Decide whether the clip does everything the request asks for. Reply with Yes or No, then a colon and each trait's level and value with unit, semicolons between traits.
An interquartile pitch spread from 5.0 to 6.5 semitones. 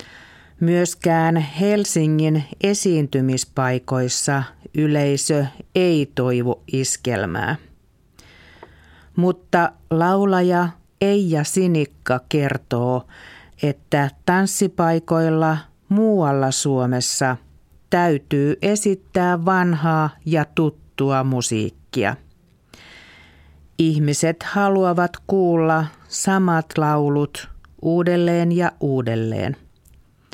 Yes: average, 5.3 semitones